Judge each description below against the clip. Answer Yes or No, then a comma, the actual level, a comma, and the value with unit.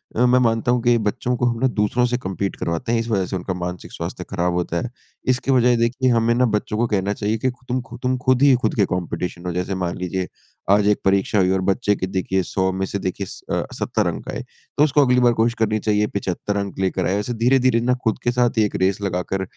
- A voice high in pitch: No, low, 105 Hz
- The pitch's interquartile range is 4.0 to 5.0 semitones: Yes, average, 4.4 semitones